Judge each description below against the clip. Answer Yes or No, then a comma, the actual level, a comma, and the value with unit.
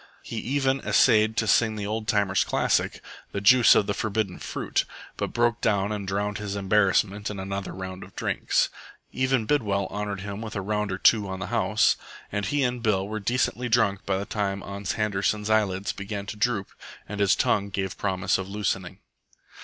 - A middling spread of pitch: No, narrow, 1.9 semitones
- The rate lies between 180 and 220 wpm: Yes, average, 190 wpm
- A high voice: No, low, 105 Hz